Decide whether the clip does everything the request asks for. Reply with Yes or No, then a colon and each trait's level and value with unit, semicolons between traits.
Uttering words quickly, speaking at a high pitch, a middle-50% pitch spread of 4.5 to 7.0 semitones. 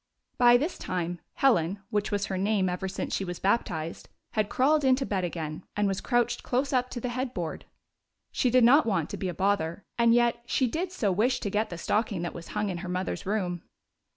Yes: fast, 225 wpm; high, 205 Hz; average, 5.1 semitones